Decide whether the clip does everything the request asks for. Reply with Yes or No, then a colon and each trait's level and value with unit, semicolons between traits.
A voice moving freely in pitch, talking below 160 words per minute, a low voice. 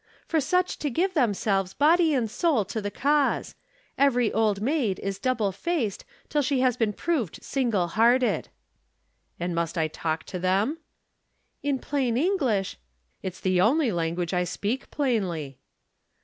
No: wide, 7.0 semitones; average, 150 wpm; high, 225 Hz